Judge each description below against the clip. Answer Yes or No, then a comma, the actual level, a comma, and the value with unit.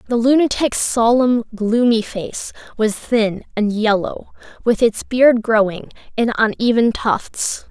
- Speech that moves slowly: Yes, slow, 125 wpm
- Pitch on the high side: Yes, high, 225 Hz